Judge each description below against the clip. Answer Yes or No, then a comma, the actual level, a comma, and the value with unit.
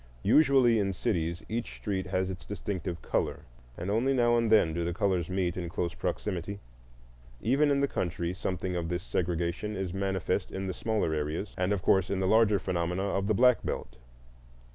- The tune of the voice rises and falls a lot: No, average, 3.5 semitones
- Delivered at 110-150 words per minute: No, average, 185 wpm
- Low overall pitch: Yes, very low, 95 Hz